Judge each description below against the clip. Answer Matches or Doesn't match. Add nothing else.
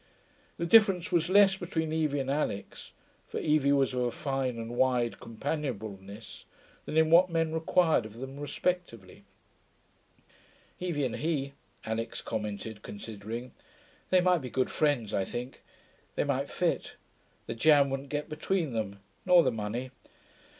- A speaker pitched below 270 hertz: Matches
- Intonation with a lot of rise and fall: Matches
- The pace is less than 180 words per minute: Matches